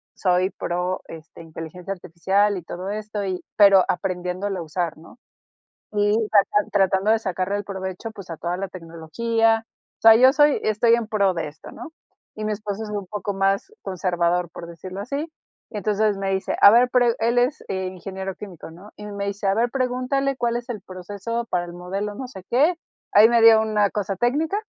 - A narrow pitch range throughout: No, average, 3.5 semitones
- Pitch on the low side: No, high, 200 Hz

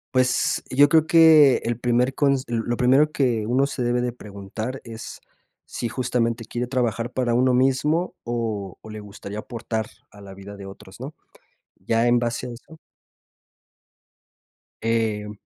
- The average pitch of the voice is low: Yes, low, 120 Hz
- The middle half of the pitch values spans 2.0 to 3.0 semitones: Yes, average, 2.7 semitones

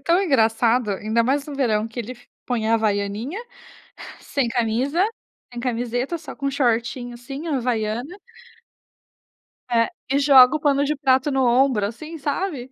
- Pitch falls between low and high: No, very high, 250 Hz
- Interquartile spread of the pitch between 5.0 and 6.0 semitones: No, average, 3.5 semitones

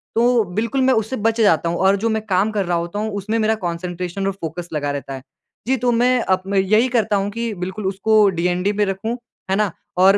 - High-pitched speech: Yes, high, 200 Hz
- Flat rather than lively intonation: No, average, 3.5 semitones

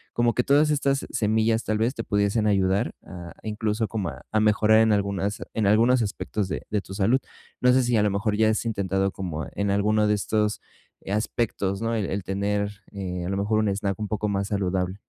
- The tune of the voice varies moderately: No, narrow, 2.1 semitones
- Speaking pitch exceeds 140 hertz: No, low, 105 Hz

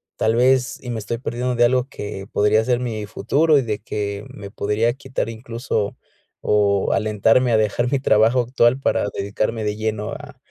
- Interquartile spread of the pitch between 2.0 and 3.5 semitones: Yes, average, 2.9 semitones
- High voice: No, low, 115 Hz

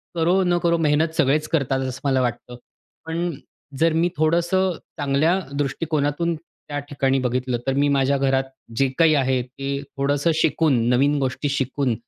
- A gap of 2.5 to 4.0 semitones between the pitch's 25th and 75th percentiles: Yes, average, 3.3 semitones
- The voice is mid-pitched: Yes, medium, 145 Hz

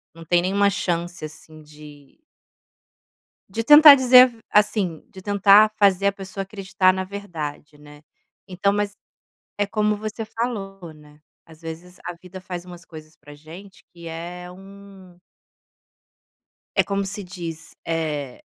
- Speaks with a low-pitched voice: No, medium, 185 Hz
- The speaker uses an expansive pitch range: No, average, 3.6 semitones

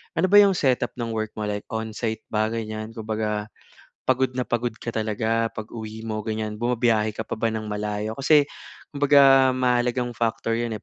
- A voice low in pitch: Yes, low, 115 Hz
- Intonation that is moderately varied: No, narrow, 2.1 semitones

